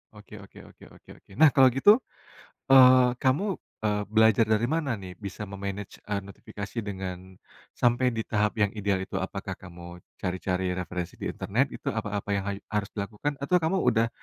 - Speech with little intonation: No, average, 4.1 semitones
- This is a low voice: Yes, low, 105 Hz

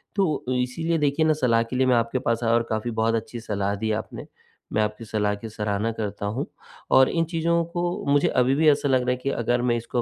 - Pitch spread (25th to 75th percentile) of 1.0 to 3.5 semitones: No, average, 4.4 semitones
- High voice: No, low, 120 Hz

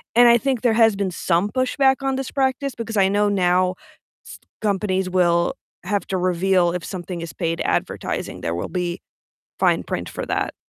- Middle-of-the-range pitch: No, high, 195 Hz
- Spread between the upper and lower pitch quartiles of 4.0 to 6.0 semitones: Yes, average, 4.6 semitones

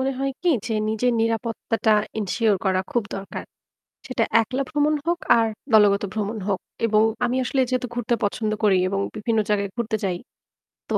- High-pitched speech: Yes, high, 225 Hz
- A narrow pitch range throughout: No, average, 3.1 semitones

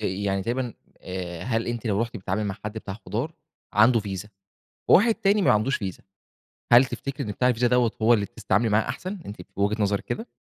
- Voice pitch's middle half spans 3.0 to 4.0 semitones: Yes, average, 3.6 semitones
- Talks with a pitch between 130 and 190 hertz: No, low, 110 Hz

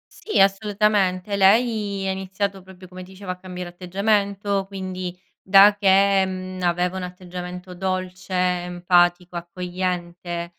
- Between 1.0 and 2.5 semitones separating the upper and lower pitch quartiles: Yes, narrow, 1.5 semitones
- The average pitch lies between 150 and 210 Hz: Yes, medium, 185 Hz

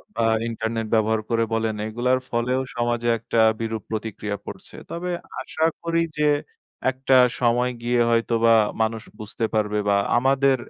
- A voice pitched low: Yes, low, 115 Hz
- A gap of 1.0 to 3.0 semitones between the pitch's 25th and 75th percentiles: Yes, narrow, 2.4 semitones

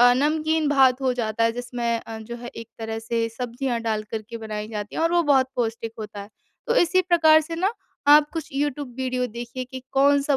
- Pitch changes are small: No, average, 4.2 semitones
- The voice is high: Yes, very high, 250 Hz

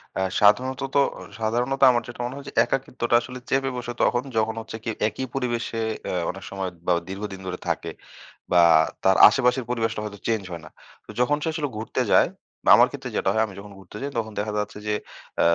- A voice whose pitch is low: Yes, low, 115 Hz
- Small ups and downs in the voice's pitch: No, average, 3.4 semitones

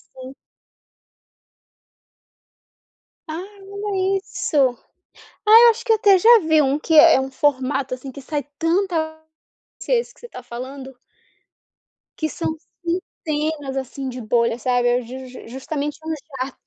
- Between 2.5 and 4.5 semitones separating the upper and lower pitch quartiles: No, average, 4.9 semitones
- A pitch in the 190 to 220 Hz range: No, very high, 290 Hz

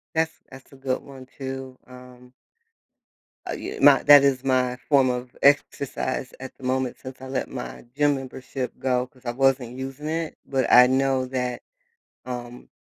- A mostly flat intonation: Yes, narrow, 1.1 semitones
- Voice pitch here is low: Yes, low, 130 Hz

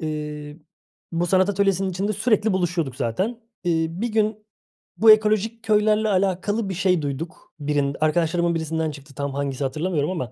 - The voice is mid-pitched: Yes, medium, 175 Hz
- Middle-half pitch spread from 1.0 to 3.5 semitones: No, wide, 5.6 semitones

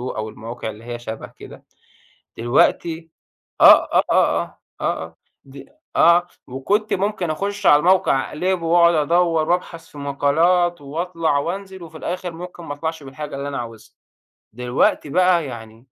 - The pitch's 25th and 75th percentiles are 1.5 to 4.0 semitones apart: No, average, 4.6 semitones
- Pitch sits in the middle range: Yes, medium, 160 Hz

